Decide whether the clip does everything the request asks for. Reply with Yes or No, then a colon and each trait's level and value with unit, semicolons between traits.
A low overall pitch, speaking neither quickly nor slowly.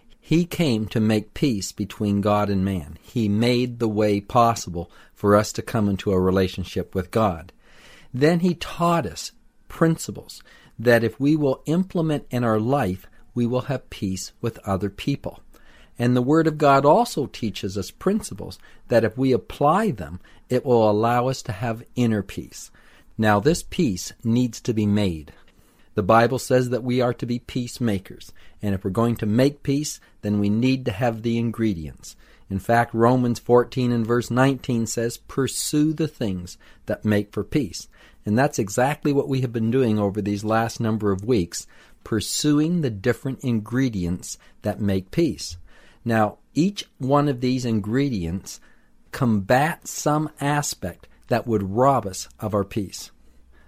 Yes: low, 115 Hz; average, 165 wpm